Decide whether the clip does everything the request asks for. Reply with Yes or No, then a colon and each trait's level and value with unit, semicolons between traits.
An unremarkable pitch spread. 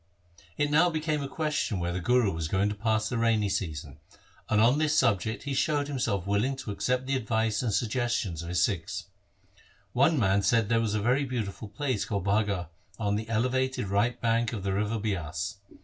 Yes: average, 4.2 semitones